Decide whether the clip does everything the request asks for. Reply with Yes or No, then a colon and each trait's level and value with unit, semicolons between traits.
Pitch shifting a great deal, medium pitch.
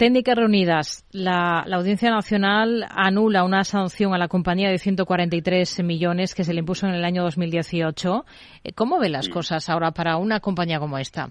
No: narrow, 2.5 semitones; medium, 180 Hz